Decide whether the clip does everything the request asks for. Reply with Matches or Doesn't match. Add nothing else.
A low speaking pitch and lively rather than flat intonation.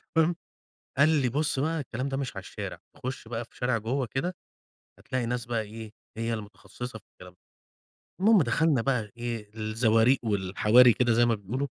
Doesn't match